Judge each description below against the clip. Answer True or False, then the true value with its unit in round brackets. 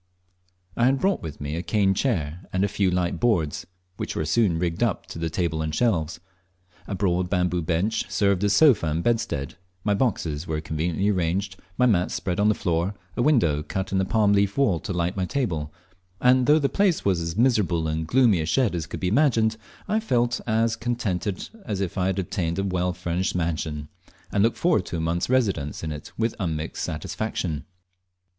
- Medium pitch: False (95 Hz)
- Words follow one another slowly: False (200 wpm)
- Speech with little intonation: False (5.1 semitones)